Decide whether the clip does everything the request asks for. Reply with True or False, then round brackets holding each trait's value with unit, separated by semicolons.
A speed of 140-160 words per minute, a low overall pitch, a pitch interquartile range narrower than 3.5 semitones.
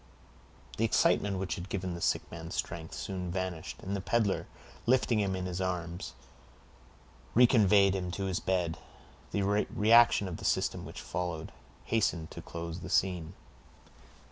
True (150 wpm; 95 Hz; 2.6 semitones)